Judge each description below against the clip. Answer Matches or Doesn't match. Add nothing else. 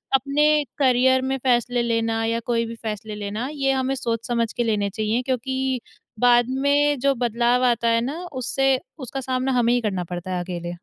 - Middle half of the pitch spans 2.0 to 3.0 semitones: Matches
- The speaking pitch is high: Matches